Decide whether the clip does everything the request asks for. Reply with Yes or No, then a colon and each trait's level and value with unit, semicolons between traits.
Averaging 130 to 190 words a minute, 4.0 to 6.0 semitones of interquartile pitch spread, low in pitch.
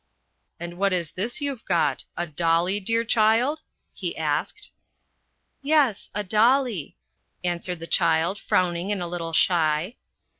No: average, 150 wpm; average, 4.9 semitones; medium, 185 Hz